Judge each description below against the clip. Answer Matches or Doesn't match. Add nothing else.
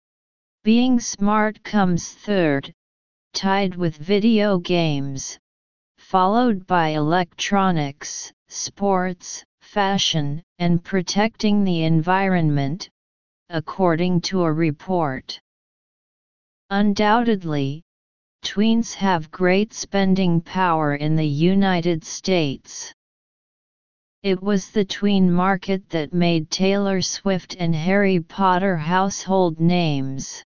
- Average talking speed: Doesn't match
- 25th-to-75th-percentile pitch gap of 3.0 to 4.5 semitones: Matches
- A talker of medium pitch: Matches